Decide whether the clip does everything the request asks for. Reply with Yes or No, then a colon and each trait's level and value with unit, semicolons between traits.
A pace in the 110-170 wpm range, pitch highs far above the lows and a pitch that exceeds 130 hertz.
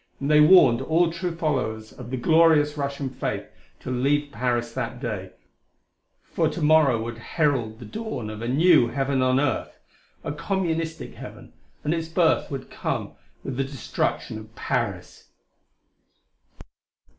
No: average, 145 wpm; average, 5.0 semitones; medium, 140 Hz